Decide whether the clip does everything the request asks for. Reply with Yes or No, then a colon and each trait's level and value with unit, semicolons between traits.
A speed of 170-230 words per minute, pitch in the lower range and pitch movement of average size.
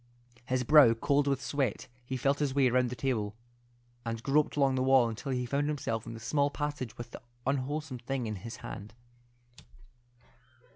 Yes: average, 180 wpm; low, 130 Hz; average, 3.2 semitones